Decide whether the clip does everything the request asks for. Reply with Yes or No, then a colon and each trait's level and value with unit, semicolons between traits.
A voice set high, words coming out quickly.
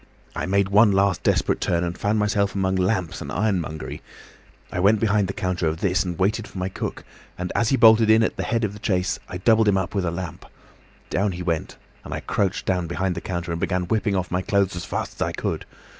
No: very low, 95 Hz; fast, 240 wpm